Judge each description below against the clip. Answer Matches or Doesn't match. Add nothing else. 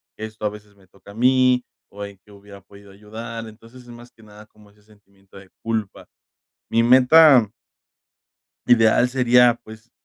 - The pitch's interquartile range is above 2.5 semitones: Matches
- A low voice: Matches